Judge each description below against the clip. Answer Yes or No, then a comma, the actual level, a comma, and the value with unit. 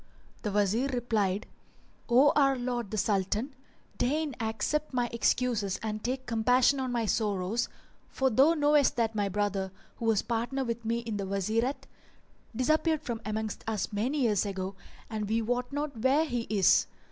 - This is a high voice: Yes, high, 230 Hz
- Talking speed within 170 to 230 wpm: No, average, 160 wpm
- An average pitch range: Yes, average, 3.7 semitones